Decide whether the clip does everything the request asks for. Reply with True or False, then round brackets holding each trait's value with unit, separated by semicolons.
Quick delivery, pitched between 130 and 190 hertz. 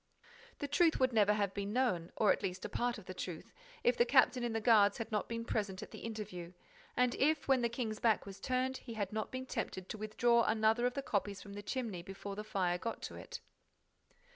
False (235 wpm; 220 Hz)